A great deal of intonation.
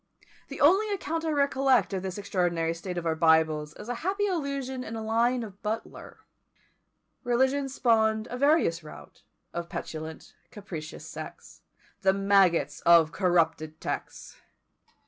Yes: wide, 7.7 semitones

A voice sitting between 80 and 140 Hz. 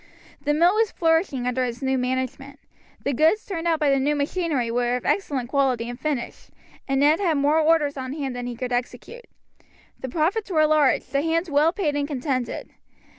No: very high, 285 Hz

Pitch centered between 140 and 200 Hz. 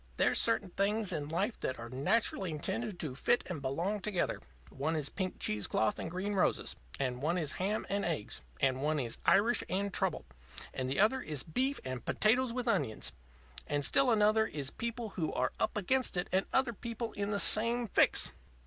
Yes: high, 190 Hz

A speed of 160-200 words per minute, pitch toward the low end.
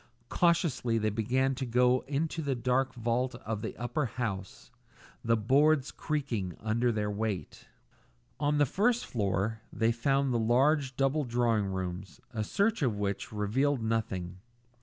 No: average, 150 wpm; low, 120 Hz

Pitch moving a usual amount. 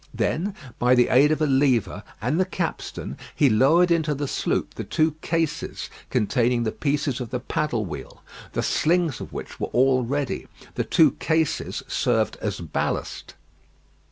Yes: average, 4.5 semitones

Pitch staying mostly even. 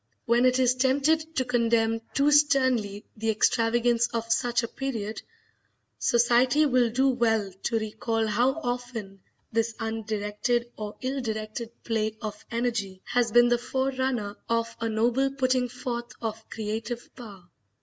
Yes: narrow, 2.2 semitones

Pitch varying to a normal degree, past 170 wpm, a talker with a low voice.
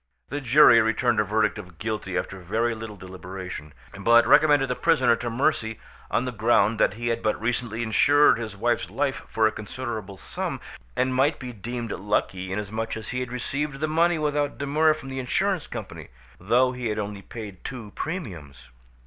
Yes: average, 4.1 semitones; average, 185 wpm; low, 115 Hz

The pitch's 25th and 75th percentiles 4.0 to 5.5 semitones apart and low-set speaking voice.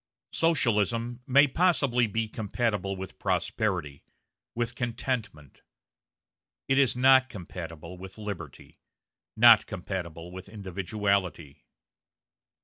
Yes: average, 4.9 semitones; low, 105 Hz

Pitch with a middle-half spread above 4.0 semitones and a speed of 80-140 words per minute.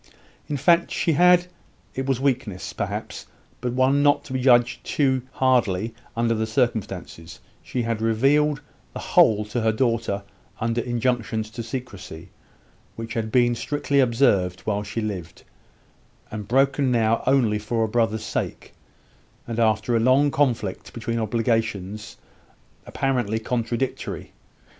No: average, 3.2 semitones; slow, 135 wpm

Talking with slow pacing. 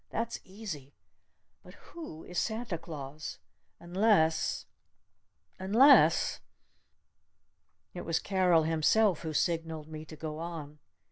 Yes: slow, 110 wpm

